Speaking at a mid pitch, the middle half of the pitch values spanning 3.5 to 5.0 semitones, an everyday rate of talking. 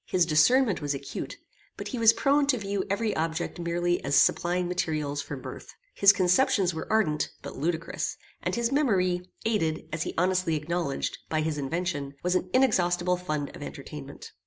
Yes: medium, 175 Hz; average, 3.9 semitones; average, 170 wpm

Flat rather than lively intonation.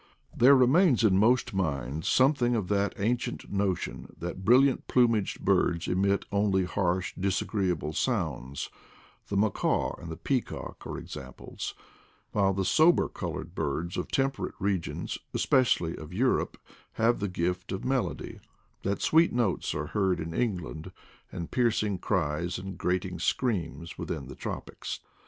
No: average, 5.2 semitones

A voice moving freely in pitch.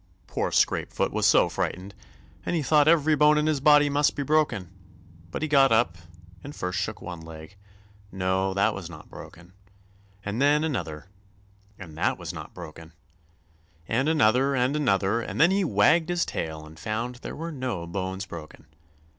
Yes: wide, 8.0 semitones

